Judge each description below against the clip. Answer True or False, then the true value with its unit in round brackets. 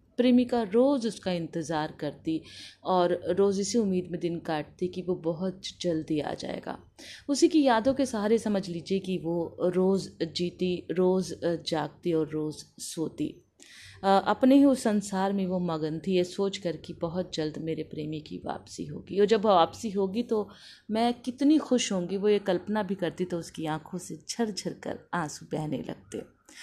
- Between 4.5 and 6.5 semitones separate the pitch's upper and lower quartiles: False (4.0 semitones)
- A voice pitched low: False (185 Hz)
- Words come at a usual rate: True (170 wpm)